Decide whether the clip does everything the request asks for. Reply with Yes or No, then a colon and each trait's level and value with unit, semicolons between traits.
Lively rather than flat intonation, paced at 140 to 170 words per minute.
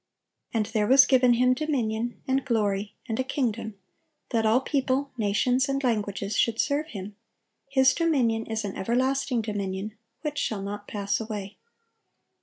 No: average, 4.0 semitones; average, 150 wpm